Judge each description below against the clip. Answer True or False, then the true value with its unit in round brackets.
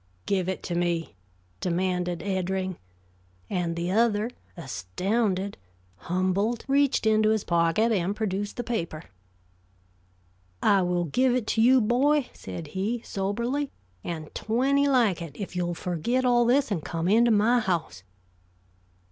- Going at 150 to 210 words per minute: False (135 wpm)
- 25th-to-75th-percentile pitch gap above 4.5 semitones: True (5.1 semitones)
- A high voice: True (200 Hz)